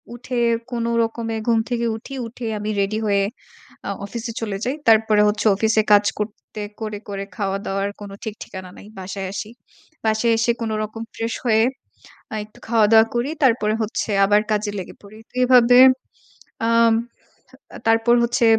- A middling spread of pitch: No, narrow, 2.0 semitones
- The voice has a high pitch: Yes, high, 220 Hz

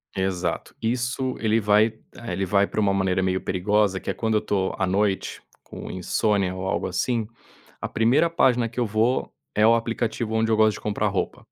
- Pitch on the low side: Yes, low, 105 Hz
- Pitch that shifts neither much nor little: Yes, average, 3.1 semitones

